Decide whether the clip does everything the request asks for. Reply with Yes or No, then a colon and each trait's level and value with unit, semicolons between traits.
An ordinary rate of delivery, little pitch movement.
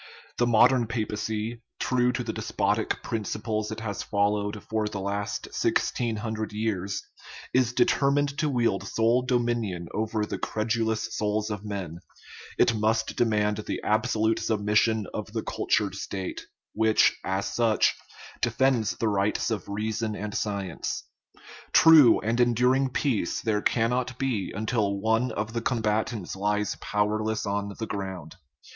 Yes: average, 150 wpm; narrow, 2.2 semitones